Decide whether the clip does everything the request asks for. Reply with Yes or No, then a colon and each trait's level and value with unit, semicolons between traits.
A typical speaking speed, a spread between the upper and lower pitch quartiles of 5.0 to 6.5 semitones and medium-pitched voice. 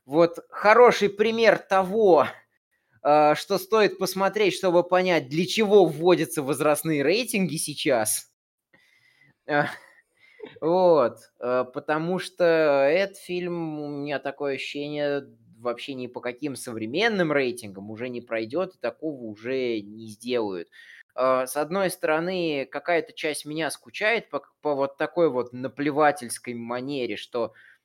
Yes: average, 125 wpm; wide, 5.4 semitones; medium, 155 Hz